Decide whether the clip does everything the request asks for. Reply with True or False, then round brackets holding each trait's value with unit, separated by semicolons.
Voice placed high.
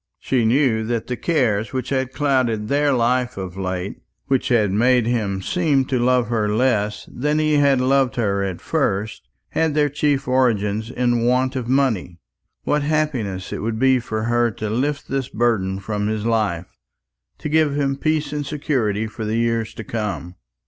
False (120 Hz)